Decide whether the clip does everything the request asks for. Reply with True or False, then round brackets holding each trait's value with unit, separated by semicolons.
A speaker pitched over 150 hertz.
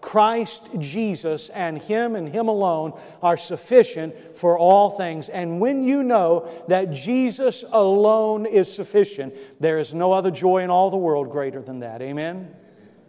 True (185 Hz)